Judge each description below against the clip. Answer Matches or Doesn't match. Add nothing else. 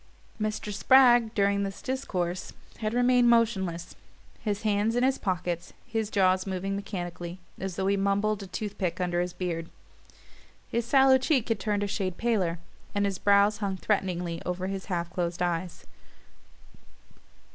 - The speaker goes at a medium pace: Matches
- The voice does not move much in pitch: Doesn't match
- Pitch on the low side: Doesn't match